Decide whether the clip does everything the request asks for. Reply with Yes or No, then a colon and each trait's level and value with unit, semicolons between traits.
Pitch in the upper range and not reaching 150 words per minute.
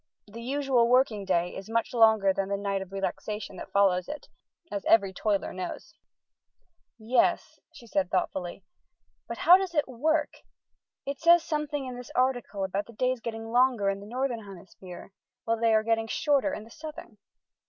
No: high, 225 Hz; average, 175 wpm